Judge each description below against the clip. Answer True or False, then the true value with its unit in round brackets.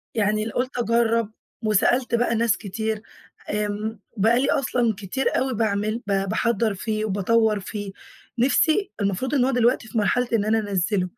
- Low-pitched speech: False (220 Hz)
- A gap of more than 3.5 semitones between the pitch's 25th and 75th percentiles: False (2.6 semitones)